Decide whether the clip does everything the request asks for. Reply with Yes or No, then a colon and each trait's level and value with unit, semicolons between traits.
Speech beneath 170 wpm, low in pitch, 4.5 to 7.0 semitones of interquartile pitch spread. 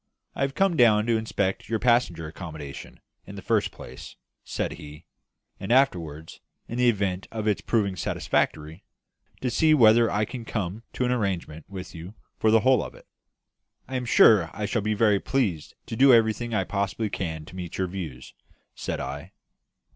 No: average, 180 wpm; low, 105 Hz; average, 4.9 semitones